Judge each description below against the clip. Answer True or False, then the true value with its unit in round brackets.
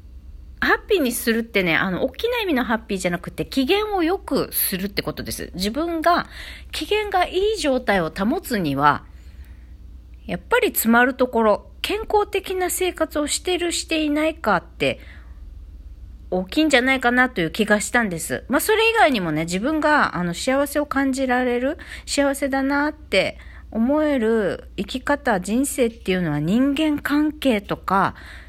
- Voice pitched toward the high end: True (250 Hz)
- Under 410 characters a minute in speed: True (320 characters per minute)